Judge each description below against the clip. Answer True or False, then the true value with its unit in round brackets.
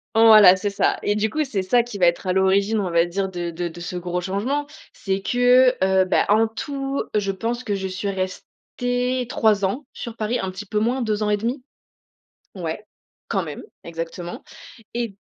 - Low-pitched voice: False (205 Hz)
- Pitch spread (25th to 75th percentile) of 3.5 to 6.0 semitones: True (4.1 semitones)